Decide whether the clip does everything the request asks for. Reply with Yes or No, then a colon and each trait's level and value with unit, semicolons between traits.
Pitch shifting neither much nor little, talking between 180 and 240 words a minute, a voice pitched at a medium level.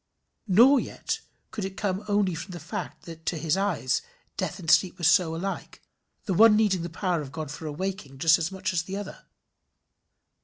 Yes: average, 3.2 semitones; average, 195 wpm; medium, 180 Hz